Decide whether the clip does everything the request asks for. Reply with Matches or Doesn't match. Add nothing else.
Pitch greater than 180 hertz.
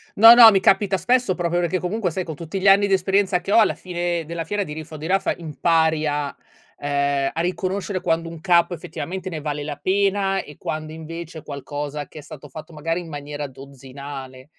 Doesn't match